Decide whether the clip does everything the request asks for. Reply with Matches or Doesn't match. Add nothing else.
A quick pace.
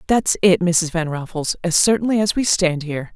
Matches